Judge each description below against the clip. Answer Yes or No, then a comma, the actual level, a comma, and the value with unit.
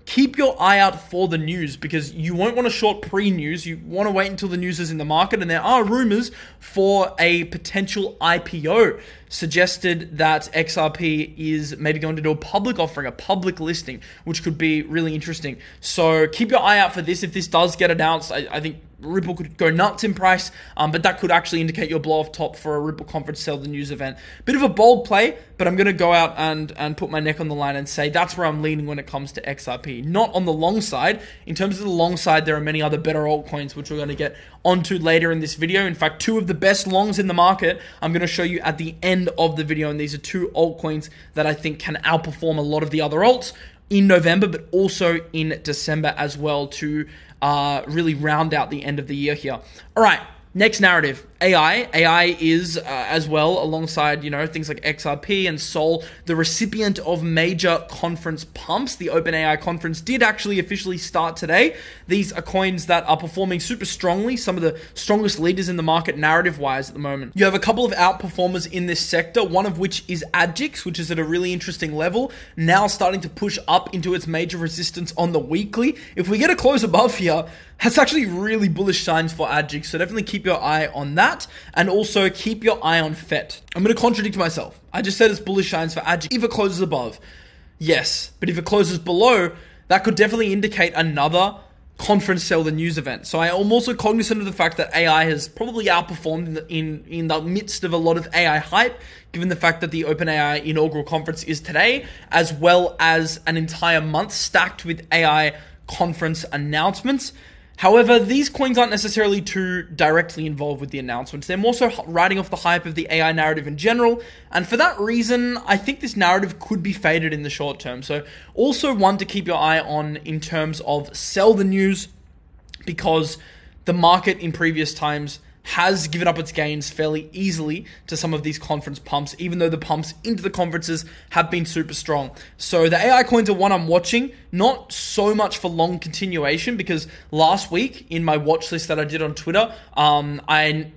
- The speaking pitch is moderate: Yes, medium, 170 Hz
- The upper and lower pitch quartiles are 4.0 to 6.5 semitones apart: No, average, 3.6 semitones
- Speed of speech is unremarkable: No, fast, 215 wpm